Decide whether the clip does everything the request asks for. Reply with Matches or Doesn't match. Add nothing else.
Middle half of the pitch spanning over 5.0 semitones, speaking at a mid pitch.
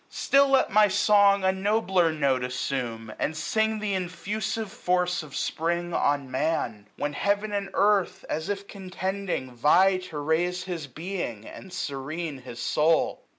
Matches